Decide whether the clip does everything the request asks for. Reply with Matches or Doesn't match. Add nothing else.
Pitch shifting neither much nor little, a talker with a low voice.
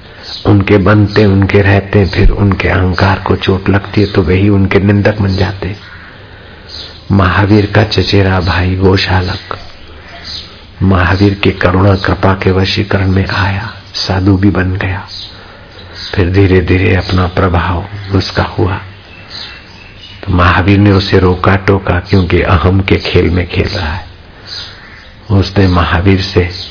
Doesn't match